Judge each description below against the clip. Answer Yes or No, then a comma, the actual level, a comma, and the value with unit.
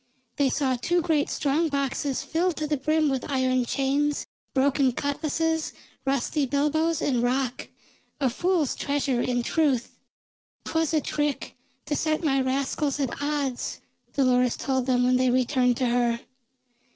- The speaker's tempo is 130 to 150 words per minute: Yes, average, 145 wpm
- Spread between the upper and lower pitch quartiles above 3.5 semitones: No, average, 2.8 semitones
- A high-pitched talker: Yes, very high, 275 Hz